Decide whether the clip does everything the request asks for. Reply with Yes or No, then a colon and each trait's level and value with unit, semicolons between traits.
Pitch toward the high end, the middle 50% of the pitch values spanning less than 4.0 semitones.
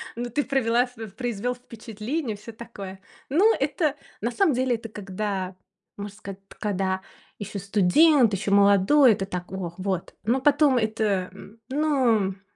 No: high, 220 Hz; average, 4.3 semitones